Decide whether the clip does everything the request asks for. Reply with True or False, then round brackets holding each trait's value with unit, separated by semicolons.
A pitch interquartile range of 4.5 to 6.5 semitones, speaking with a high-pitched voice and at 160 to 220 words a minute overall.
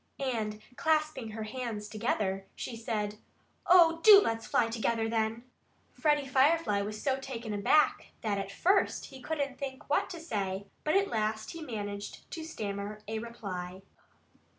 False (5.2 semitones; 225 Hz; 150 wpm)